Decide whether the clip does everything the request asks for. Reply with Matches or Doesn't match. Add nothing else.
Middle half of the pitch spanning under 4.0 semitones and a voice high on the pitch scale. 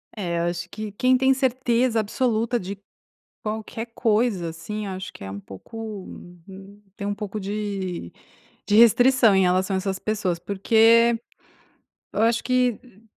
Matches